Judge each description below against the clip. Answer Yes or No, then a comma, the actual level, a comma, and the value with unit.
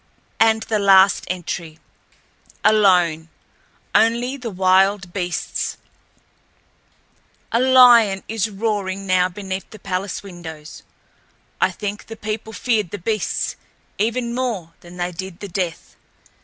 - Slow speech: Yes, slow, 120 wpm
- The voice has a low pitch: No, high, 195 Hz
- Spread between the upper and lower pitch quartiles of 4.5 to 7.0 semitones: No, average, 3.6 semitones